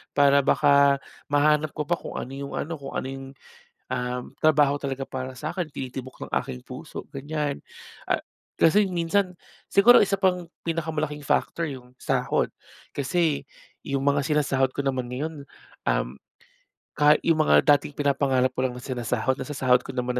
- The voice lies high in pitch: No, medium, 140 Hz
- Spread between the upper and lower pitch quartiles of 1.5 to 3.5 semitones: Yes, average, 2.9 semitones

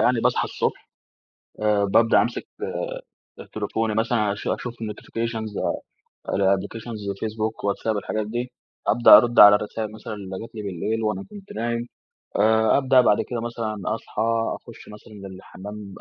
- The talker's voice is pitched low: Yes, low, 110 Hz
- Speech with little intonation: Yes, narrow, 2.0 semitones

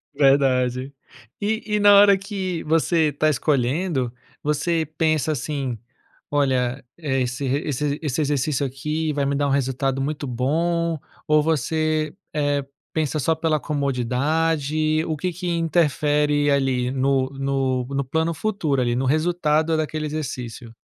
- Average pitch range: Yes, average, 3.0 semitones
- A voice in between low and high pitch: Yes, medium, 150 Hz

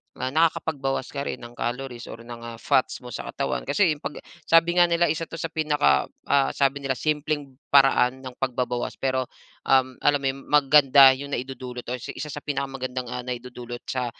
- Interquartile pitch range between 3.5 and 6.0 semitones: No, average, 2.7 semitones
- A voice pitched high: No, low, 135 Hz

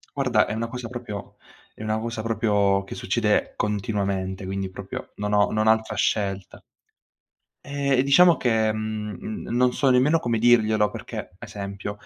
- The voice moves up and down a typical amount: Yes, average, 3.0 semitones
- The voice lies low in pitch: Yes, low, 110 Hz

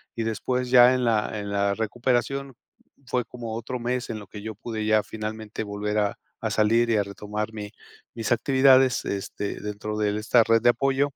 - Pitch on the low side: Yes, low, 110 Hz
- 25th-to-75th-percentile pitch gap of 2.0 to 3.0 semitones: Yes, average, 2.7 semitones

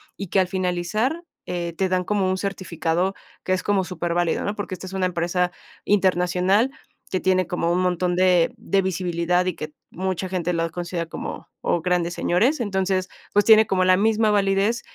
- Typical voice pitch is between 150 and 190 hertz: Yes, medium, 185 Hz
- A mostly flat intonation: Yes, narrow, 1.8 semitones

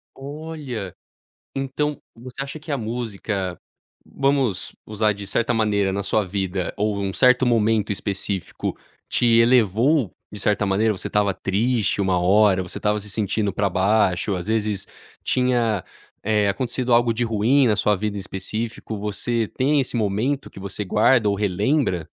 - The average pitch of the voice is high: No, low, 105 Hz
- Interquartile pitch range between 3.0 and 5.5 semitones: Yes, average, 3.6 semitones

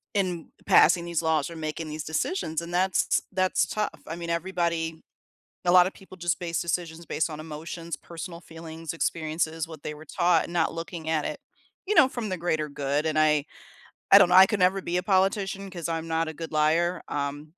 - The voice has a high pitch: No, medium, 170 Hz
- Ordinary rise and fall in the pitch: No, narrow, 2.2 semitones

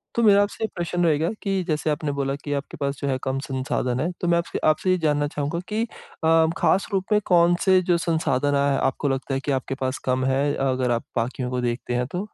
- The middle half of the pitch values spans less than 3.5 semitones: No, average, 4.6 semitones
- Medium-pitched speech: Yes, medium, 145 Hz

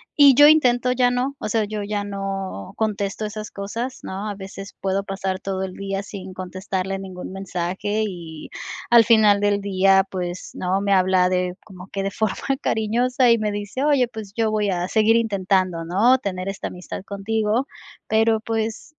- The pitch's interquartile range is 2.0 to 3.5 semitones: Yes, average, 2.7 semitones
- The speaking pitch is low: No, high, 200 Hz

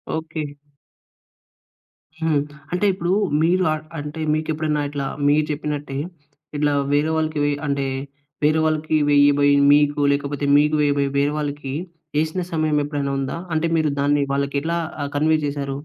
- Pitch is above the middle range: No, medium, 150 Hz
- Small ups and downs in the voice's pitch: Yes, narrow, 1.6 semitones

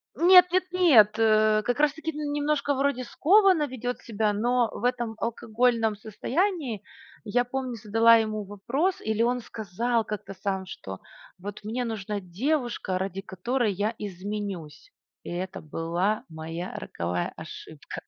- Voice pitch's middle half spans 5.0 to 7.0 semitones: No, average, 4.2 semitones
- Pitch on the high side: Yes, high, 220 Hz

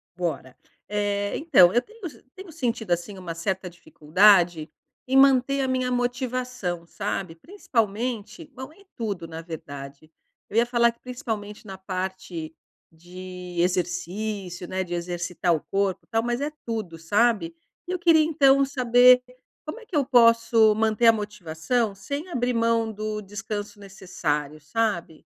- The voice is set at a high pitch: Yes, high, 210 Hz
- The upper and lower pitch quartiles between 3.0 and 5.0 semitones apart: No, wide, 5.6 semitones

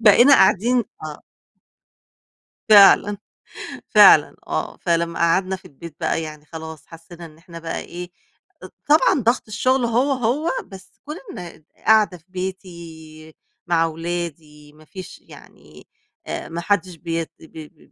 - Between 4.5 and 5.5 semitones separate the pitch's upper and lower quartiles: No, average, 4.1 semitones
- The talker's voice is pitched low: No, medium, 170 Hz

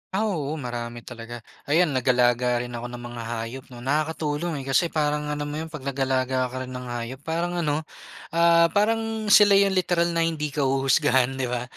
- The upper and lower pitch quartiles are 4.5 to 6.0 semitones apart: Yes, average, 4.9 semitones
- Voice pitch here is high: No, medium, 140 Hz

